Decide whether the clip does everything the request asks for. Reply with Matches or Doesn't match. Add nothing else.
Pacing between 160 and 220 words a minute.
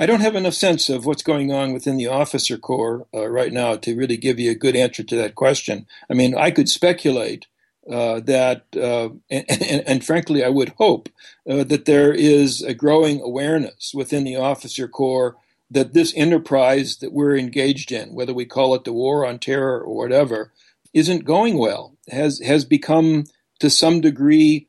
Matches